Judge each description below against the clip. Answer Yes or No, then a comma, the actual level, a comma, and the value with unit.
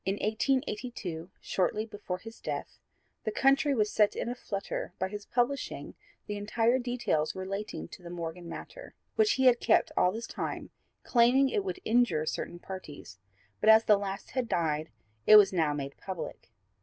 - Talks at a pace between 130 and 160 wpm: No, average, 170 wpm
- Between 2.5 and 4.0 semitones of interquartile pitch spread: No, average, 5.2 semitones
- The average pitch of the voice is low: No, high, 210 Hz